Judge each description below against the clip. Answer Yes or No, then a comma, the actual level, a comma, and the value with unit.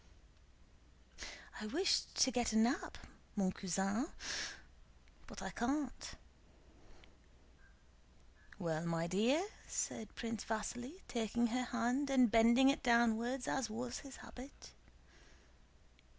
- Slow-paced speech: Yes, slow, 105 wpm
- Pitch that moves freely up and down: No, average, 3.1 semitones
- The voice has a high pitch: Yes, high, 235 Hz